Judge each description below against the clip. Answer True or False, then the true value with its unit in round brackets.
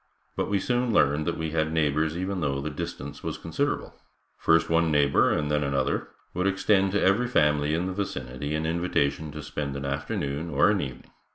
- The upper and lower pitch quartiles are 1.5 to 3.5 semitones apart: False (4.1 semitones)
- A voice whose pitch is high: False (75 Hz)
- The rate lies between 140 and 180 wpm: False (195 wpm)